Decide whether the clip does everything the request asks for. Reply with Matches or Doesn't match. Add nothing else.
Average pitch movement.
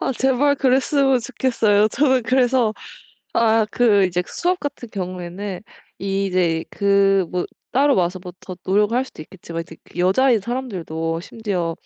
Doesn't match